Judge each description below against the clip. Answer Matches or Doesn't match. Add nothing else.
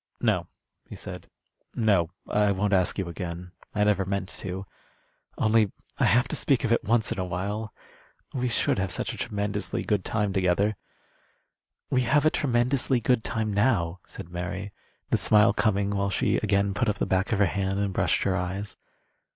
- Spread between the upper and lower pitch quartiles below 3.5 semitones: Matches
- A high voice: Doesn't match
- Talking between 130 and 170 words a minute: Doesn't match